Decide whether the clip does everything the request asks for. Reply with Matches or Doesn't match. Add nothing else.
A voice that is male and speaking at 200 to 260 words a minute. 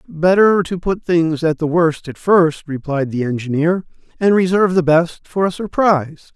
Doesn't match